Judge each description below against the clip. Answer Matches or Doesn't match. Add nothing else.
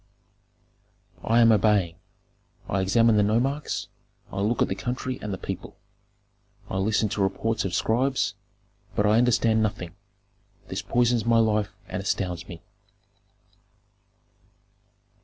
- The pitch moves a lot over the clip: Doesn't match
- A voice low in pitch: Matches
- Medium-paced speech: Doesn't match